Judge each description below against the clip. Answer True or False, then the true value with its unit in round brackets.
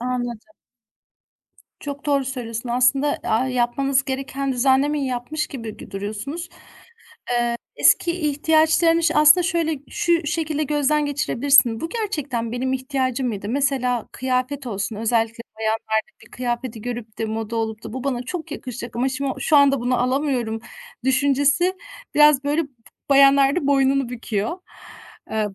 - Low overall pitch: False (265 Hz)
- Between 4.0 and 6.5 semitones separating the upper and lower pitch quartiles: False (3.4 semitones)